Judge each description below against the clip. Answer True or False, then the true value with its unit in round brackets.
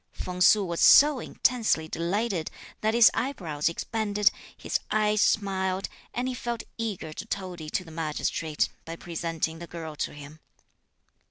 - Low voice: False (185 Hz)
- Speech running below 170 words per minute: True (150 wpm)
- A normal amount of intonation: True (4.9 semitones)